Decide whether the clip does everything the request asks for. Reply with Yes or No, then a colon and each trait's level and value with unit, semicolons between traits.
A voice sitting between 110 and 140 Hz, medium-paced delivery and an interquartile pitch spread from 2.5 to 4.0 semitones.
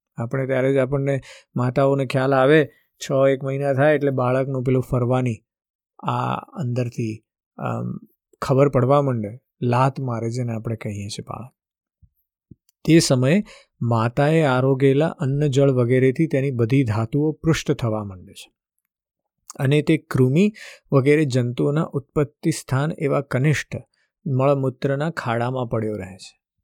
Yes: low, 135 Hz; average, 125 wpm; average, 2.8 semitones